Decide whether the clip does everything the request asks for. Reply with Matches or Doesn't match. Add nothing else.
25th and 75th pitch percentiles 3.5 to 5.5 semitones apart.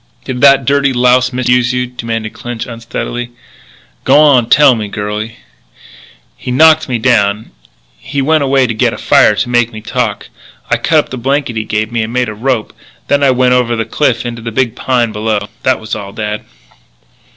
Doesn't match